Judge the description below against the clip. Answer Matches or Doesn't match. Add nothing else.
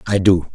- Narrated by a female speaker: Doesn't match